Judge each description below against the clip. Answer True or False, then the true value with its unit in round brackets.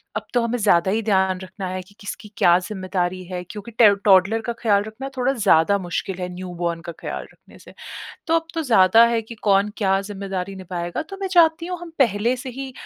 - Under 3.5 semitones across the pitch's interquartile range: False (4.0 semitones)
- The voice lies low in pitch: False (200 Hz)